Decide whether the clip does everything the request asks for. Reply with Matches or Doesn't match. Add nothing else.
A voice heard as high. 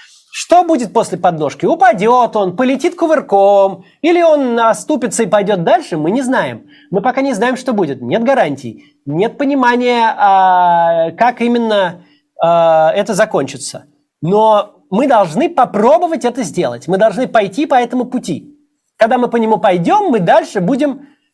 Matches